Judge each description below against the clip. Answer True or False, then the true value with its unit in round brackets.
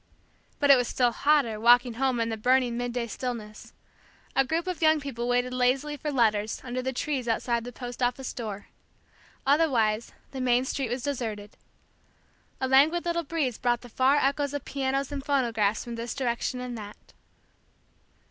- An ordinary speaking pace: True (170 wpm)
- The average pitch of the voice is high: True (250 Hz)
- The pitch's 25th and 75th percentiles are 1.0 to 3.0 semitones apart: True (2.7 semitones)